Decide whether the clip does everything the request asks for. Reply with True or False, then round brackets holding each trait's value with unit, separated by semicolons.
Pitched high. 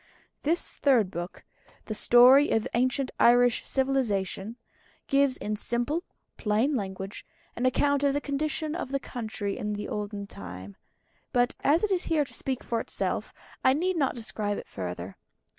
True (245 Hz)